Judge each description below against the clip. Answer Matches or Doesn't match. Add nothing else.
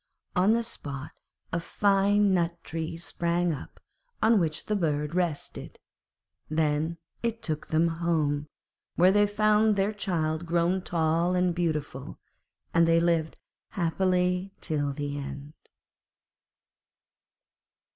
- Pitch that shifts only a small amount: Doesn't match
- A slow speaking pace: Matches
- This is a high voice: Doesn't match